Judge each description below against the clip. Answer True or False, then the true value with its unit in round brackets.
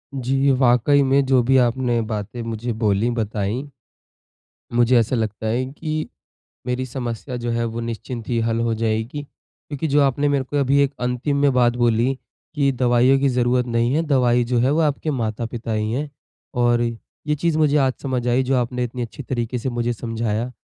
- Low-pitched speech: True (125 Hz)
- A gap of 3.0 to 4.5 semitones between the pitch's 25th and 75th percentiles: False (2.6 semitones)